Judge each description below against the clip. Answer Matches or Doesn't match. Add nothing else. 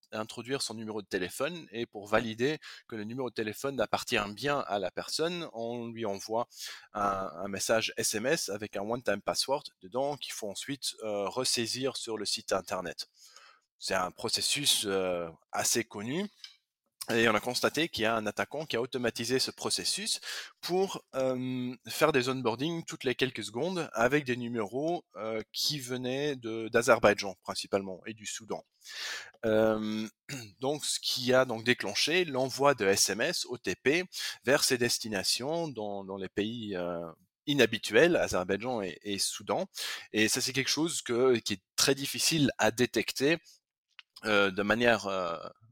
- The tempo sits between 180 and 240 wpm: Doesn't match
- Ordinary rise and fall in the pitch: Matches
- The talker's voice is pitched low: Matches